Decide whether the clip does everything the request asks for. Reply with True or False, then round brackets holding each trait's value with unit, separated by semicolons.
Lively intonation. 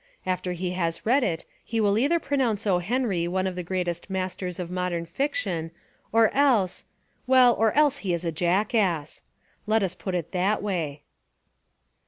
False (4.2 semitones)